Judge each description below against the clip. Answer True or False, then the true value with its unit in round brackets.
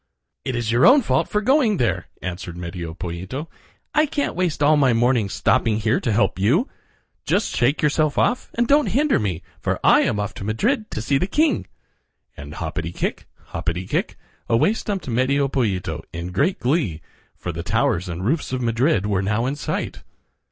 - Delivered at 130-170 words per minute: False (185 wpm)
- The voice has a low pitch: True (120 Hz)